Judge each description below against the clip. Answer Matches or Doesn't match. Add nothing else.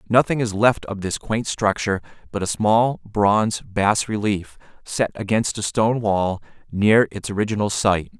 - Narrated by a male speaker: Matches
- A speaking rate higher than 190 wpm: Doesn't match